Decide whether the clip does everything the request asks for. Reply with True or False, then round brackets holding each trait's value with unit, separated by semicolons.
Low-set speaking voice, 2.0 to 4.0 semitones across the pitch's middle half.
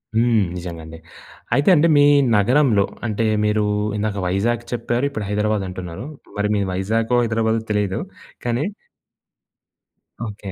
True (105 Hz; 3.1 semitones)